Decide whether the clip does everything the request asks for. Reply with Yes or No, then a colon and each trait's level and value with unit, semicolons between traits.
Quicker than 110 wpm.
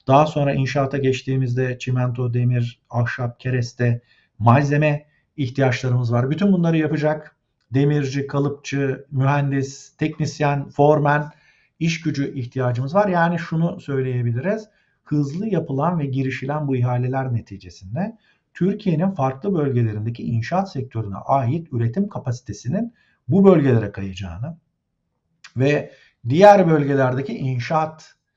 No: average, 100 wpm